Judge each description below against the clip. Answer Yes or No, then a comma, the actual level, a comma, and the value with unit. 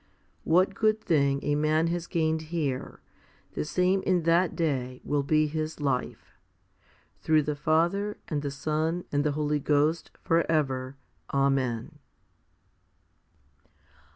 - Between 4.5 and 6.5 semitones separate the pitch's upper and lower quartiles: No, average, 2.8 semitones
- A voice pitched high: No, medium, 155 Hz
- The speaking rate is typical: No, slow, 125 wpm